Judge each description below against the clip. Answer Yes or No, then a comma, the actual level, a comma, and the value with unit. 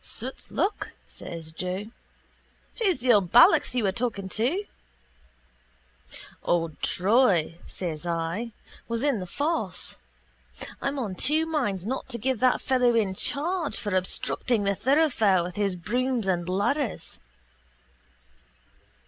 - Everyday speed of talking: No, slow, 125 wpm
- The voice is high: Yes, high, 225 Hz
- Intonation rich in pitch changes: Yes, wide, 6.0 semitones